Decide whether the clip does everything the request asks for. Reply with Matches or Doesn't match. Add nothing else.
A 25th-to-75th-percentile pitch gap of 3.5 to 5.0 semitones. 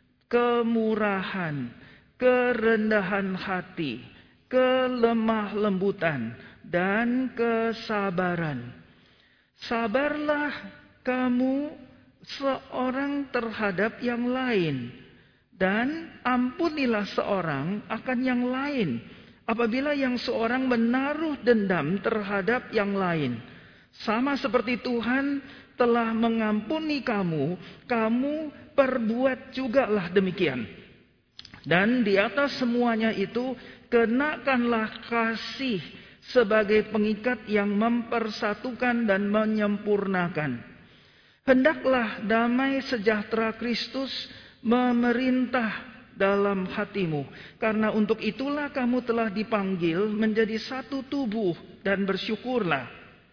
Matches